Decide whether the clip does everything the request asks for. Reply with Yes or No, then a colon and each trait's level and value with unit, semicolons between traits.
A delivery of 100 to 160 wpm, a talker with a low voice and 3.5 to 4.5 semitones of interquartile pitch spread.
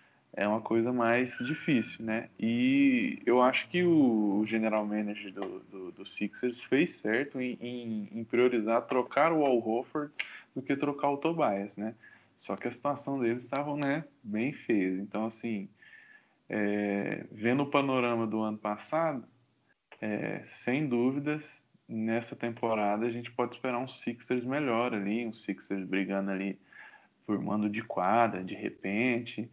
Yes: average, 150 wpm; low, 120 Hz; average, 4.2 semitones